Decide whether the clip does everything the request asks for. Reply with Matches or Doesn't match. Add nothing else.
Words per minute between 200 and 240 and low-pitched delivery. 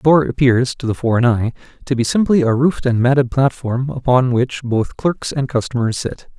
Matches